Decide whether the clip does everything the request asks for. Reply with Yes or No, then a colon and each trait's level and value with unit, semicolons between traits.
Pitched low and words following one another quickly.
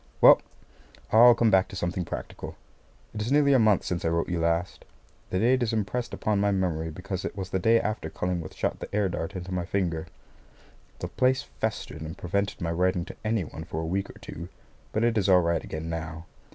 Yes: very low, 95 Hz; fast, 225 wpm